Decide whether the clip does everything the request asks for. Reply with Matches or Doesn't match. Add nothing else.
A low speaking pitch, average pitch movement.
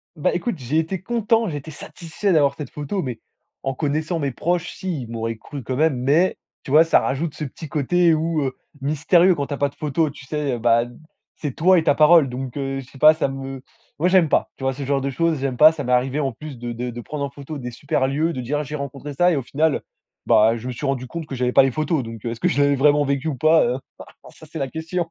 Doesn't match